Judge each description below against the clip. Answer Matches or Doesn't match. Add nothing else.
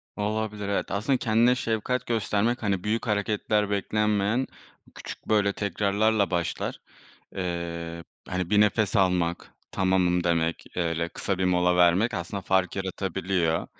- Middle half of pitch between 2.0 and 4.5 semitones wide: Matches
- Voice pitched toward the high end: Doesn't match